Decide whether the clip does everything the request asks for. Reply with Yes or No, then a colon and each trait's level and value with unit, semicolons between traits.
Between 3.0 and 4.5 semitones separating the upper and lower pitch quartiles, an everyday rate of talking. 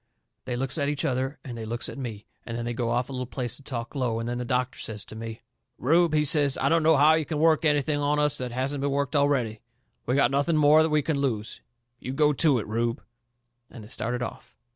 No: average, 3.7 semitones; fast, 250 wpm